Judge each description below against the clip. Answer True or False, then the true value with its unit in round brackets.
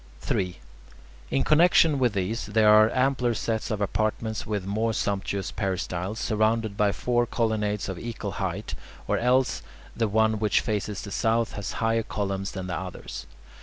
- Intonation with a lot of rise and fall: False (2.4 semitones)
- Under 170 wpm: True (160 wpm)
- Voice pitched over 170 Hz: False (110 Hz)